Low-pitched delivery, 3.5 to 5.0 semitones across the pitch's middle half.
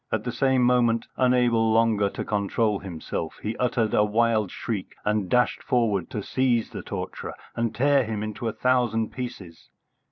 No: low, 115 Hz; average, 2.8 semitones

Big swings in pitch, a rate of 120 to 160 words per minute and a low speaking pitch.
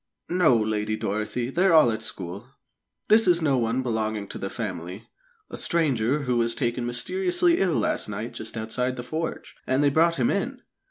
No: wide, 6.6 semitones; average, 180 wpm; low, 125 Hz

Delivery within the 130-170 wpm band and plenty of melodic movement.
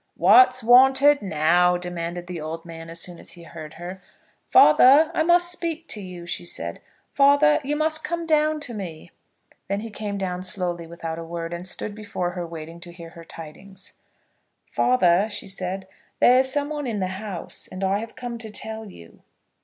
No: average, 190 wpm; wide, 6.7 semitones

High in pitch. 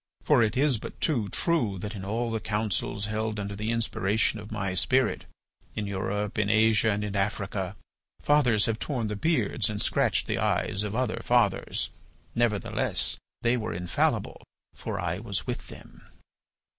No: low, 105 Hz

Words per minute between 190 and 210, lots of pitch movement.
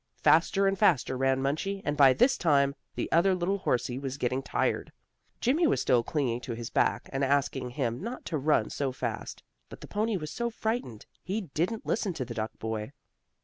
Yes: average, 195 wpm; wide, 7.3 semitones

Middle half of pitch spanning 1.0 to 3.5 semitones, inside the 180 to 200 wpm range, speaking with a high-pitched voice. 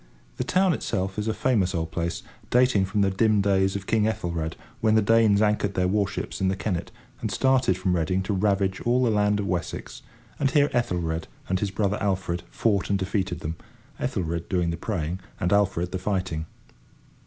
No: average, 3.0 semitones; average, 190 wpm; very low, 95 Hz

